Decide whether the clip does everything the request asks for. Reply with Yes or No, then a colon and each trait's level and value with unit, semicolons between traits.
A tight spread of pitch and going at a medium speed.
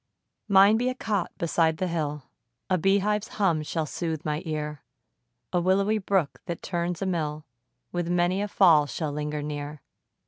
No: average, 4.2 semitones; average, 170 wpm